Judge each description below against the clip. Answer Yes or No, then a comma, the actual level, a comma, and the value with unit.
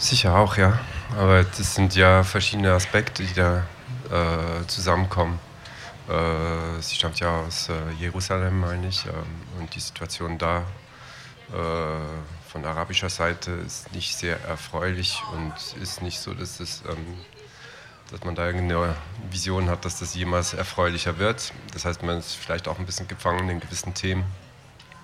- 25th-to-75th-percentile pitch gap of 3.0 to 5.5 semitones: No, narrow, 2.5 semitones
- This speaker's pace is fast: No, average, 155 wpm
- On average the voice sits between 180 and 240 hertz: No, very low, 90 Hz